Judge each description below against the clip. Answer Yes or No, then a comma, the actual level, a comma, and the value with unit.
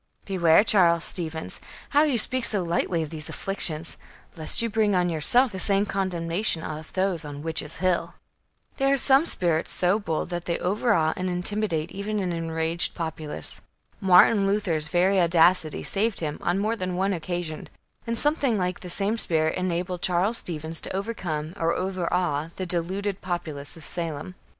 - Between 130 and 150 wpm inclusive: No, average, 165 wpm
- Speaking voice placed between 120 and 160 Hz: No, medium, 180 Hz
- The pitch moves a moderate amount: Yes, average, 3.4 semitones